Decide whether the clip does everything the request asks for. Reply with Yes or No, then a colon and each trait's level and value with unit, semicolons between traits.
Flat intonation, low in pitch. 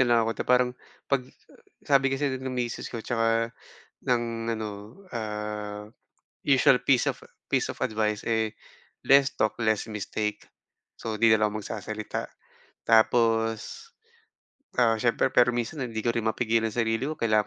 Yes: narrow, 2.2 semitones; low, 115 Hz